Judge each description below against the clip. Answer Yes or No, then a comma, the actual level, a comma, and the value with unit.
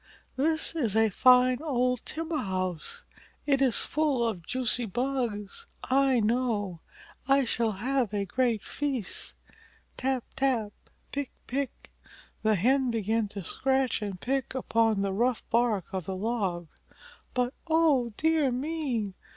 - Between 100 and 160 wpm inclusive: Yes, slow, 135 wpm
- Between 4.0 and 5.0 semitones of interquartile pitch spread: Yes, average, 4.3 semitones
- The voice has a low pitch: No, high, 245 Hz